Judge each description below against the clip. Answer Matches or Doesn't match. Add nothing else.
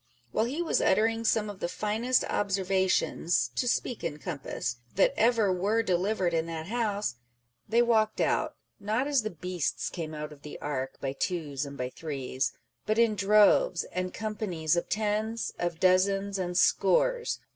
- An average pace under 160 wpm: Doesn't match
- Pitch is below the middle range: Doesn't match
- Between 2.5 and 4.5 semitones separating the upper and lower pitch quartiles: Doesn't match